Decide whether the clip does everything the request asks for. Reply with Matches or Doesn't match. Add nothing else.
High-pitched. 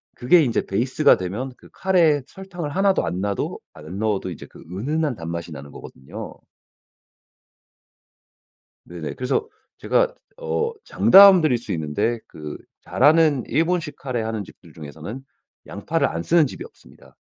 Doesn't match